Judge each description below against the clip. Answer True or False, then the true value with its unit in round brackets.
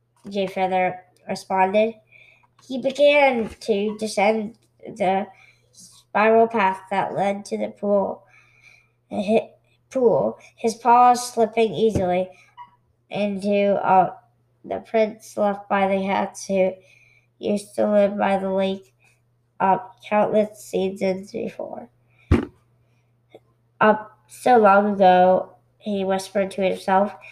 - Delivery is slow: True (105 wpm)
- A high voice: True (195 Hz)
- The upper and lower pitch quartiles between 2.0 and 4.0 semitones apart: True (2.7 semitones)